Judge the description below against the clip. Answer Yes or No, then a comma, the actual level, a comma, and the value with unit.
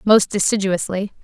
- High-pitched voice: Yes, high, 195 Hz